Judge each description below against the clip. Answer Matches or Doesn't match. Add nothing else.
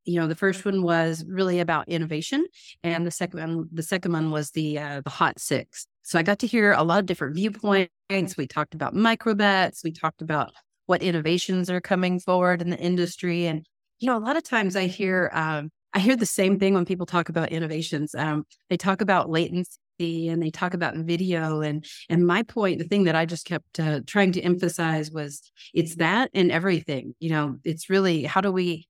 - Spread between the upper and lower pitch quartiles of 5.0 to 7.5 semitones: Doesn't match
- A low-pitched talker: Doesn't match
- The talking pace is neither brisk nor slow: Doesn't match